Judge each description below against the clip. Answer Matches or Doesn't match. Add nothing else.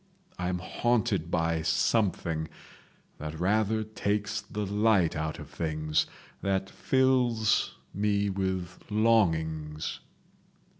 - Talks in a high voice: Doesn't match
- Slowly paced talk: Matches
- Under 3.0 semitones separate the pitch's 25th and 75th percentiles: Doesn't match